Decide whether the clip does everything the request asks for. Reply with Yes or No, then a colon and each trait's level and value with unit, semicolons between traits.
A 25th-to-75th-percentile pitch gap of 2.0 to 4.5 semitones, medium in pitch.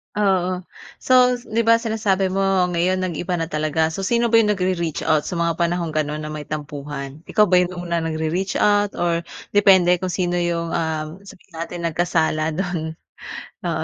Yes: average, 2.9 semitones; medium, 175 Hz